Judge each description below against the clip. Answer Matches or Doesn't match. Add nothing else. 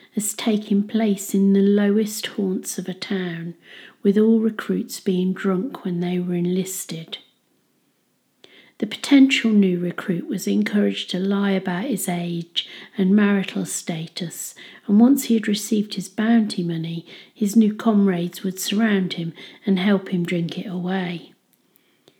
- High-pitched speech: Matches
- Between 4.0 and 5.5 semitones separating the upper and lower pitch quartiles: Doesn't match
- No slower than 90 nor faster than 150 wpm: Matches